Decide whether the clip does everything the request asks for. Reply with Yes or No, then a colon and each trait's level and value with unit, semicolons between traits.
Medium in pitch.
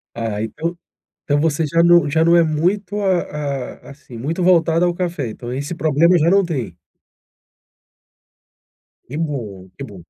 Yes: medium, 155 Hz